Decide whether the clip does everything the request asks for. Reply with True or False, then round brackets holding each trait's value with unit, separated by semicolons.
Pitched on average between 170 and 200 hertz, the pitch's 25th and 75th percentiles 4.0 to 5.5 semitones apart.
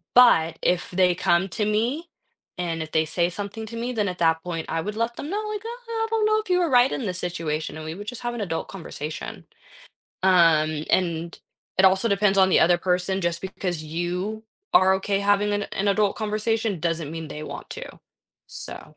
True (190 Hz; 4.6 semitones)